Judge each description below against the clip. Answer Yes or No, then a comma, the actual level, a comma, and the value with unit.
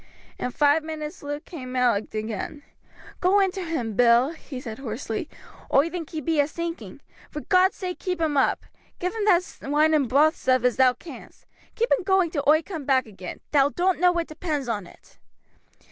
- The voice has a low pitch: No, very high, 300 Hz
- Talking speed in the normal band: Yes, average, 195 wpm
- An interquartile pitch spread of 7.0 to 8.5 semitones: No, average, 5.3 semitones